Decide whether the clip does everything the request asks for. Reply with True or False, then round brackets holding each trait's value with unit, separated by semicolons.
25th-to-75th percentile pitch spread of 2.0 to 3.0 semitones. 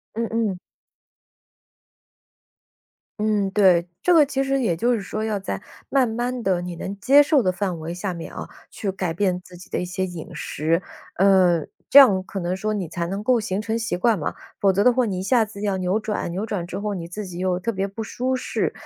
False (3.8 semitones)